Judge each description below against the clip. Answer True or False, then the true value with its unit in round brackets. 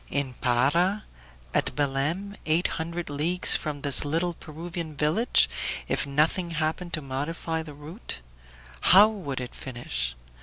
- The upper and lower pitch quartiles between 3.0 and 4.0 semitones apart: True (3.5 semitones)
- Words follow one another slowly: True (130 wpm)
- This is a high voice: False (155 Hz)